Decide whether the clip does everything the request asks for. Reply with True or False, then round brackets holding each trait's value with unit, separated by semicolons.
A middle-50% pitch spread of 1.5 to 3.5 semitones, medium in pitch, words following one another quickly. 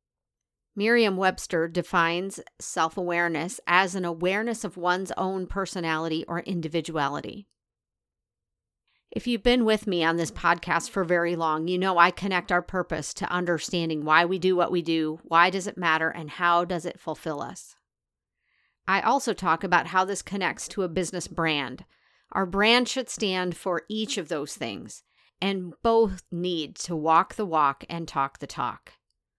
False (2.6 semitones; 175 Hz; 160 wpm)